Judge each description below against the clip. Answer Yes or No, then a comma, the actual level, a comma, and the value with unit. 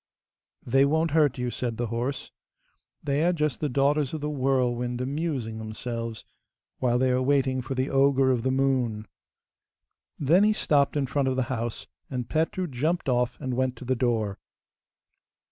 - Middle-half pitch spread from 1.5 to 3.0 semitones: Yes, average, 2.7 semitones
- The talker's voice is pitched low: Yes, low, 130 Hz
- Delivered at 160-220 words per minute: Yes, average, 170 wpm